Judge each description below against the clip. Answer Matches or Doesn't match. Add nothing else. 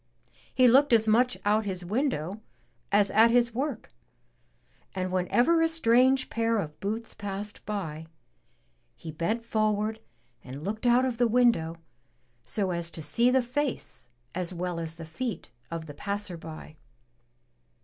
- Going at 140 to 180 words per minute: Matches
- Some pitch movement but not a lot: Doesn't match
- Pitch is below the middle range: Doesn't match